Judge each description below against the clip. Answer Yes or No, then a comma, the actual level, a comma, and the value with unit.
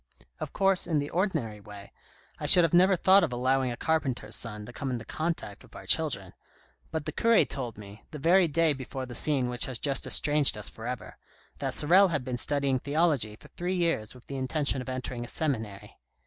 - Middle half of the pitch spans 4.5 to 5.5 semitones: Yes, average, 5.1 semitones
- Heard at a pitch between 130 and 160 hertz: Yes, low, 135 Hz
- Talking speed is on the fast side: Yes, fast, 210 wpm